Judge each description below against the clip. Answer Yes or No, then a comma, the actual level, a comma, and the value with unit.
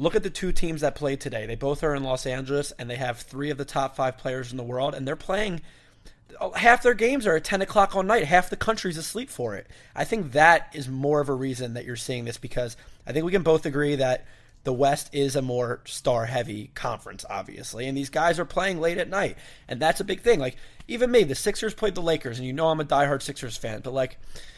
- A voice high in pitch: No, medium, 140 Hz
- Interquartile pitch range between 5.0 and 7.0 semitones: Yes, wide, 5.4 semitones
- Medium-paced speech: No, fast, 255 wpm